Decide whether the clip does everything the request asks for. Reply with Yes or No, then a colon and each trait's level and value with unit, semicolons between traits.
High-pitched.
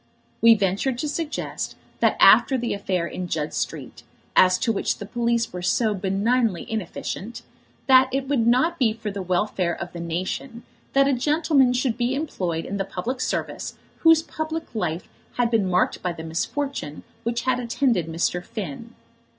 Yes: high, 225 Hz